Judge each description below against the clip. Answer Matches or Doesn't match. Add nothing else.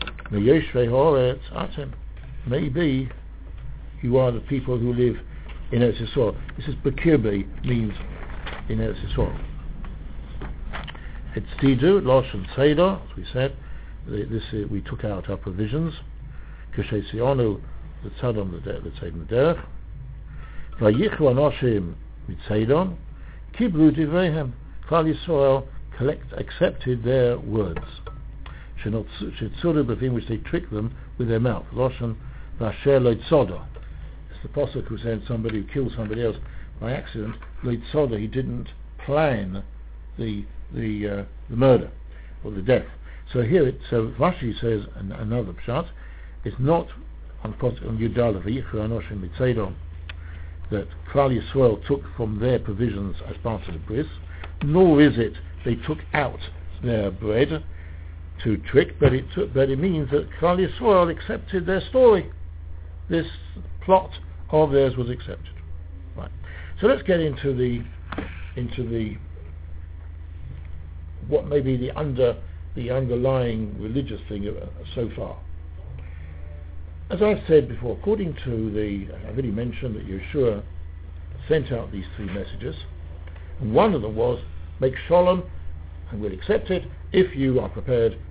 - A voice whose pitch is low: Matches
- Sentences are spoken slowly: Matches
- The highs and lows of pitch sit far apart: Matches